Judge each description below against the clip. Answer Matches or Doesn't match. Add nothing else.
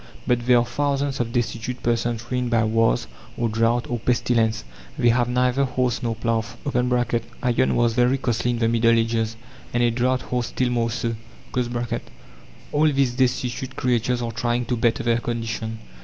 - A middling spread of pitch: Doesn't match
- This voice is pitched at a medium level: Doesn't match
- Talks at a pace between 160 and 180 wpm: Matches